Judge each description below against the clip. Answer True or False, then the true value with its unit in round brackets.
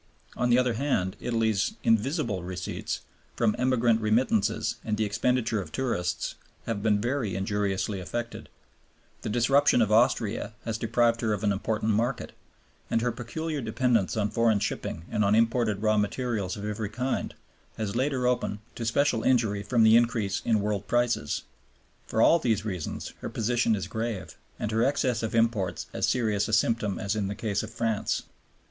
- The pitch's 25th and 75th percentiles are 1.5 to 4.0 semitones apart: True (2.6 semitones)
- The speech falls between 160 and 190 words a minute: True (170 wpm)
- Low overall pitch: True (110 Hz)